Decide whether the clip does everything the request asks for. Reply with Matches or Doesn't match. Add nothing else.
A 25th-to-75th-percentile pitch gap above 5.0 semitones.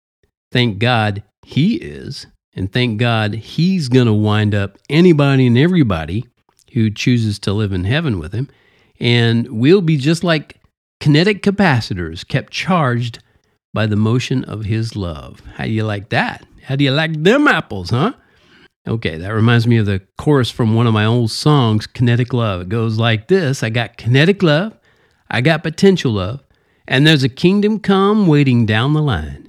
Matches